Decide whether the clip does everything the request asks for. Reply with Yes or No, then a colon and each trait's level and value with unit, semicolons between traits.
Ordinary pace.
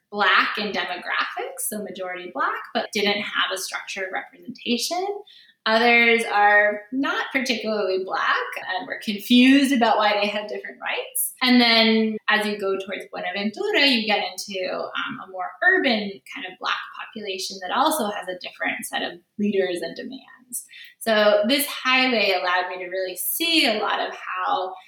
Yes: average, 160 wpm